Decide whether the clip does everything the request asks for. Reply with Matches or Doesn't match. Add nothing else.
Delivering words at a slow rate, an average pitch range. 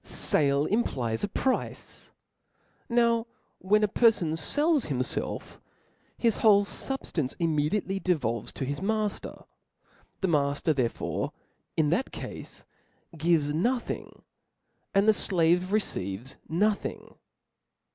Doesn't match